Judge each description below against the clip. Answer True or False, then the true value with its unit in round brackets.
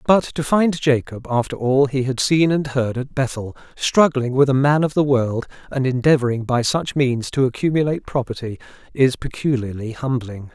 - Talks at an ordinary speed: True (175 wpm)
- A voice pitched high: False (130 Hz)